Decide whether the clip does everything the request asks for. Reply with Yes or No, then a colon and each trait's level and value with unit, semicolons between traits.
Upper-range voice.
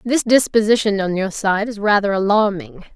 Yes: high, 205 Hz